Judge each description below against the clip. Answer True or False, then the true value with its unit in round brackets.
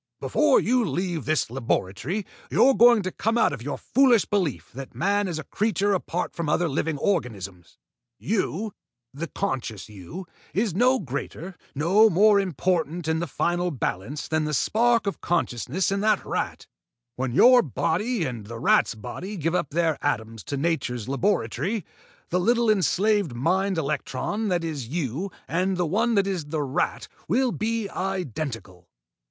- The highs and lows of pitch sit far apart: True (6.6 semitones)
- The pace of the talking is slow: False (160 wpm)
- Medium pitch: True (175 Hz)